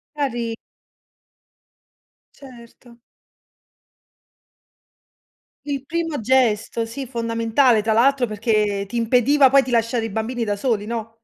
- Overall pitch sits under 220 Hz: No, high, 235 Hz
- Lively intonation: No, average, 2.8 semitones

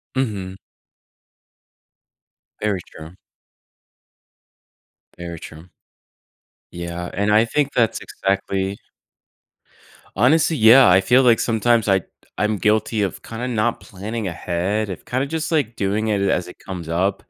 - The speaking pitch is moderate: No, low, 105 Hz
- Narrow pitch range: No, average, 3.9 semitones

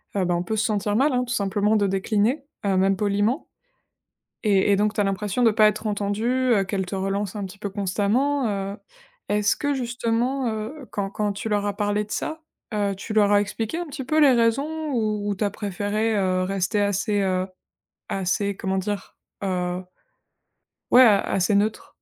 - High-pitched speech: Yes, high, 205 Hz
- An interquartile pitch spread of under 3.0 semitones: Yes, narrow, 2.5 semitones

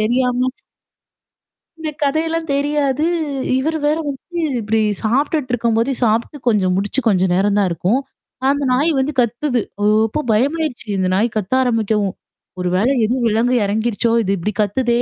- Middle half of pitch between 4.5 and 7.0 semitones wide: Yes, average, 4.8 semitones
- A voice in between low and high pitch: No, high, 240 Hz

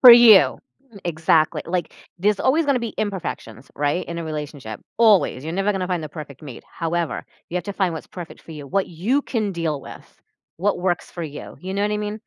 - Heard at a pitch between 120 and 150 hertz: No, medium, 175 Hz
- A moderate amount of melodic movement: Yes, average, 4.6 semitones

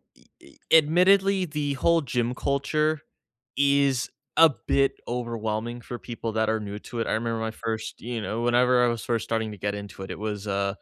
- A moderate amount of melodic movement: Yes, average, 4.1 semitones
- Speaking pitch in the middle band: No, low, 120 Hz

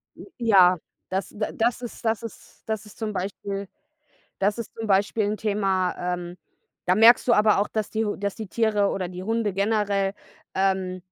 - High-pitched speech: Yes, high, 205 Hz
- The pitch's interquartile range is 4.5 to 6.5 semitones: No, narrow, 2.5 semitones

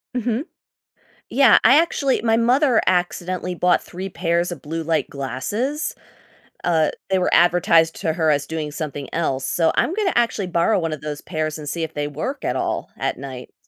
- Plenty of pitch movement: Yes, wide, 6.3 semitones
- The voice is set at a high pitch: No, medium, 170 Hz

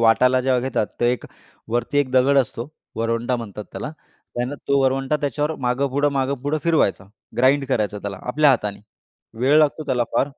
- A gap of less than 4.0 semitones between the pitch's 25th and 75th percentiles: Yes, average, 2.7 semitones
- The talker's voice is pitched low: Yes, low, 130 Hz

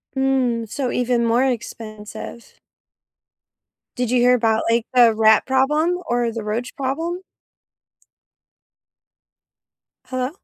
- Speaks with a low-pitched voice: No, high, 245 Hz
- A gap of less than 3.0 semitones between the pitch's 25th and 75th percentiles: Yes, narrow, 2.5 semitones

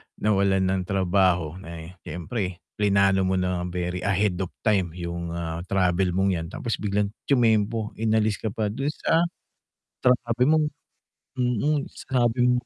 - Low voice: Yes, low, 100 Hz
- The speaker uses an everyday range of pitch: Yes, average, 3.8 semitones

